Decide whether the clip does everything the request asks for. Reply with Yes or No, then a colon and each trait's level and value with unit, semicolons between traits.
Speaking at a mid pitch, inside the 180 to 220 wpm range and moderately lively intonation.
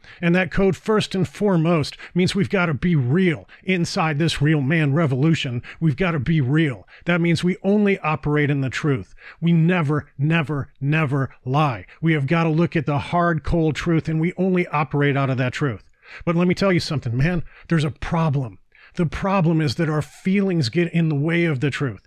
Yes: medium, 160 Hz; fast, 205 wpm; average, 3.2 semitones